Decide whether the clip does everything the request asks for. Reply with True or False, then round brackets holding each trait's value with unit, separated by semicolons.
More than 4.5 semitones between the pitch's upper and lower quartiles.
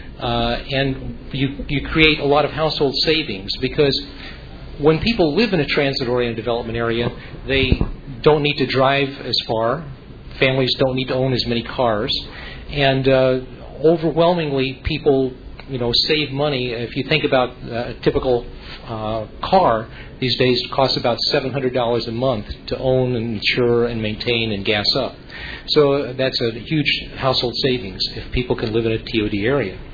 False (3.0 semitones)